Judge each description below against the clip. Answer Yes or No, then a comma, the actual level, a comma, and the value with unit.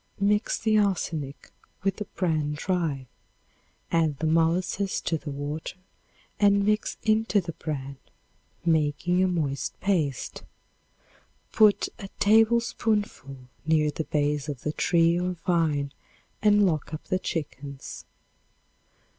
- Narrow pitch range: No, average, 5.1 semitones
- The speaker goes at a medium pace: No, slow, 120 wpm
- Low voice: No, medium, 165 Hz